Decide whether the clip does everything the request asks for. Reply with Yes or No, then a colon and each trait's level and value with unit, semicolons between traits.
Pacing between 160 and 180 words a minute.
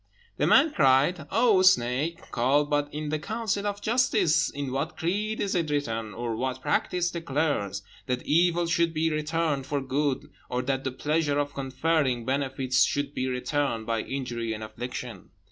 Yes: average, 165 wpm